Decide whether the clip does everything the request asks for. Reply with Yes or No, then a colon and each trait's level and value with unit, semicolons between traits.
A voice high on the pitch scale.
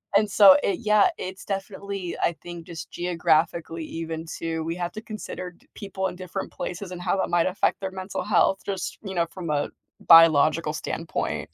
No: medium, 180 Hz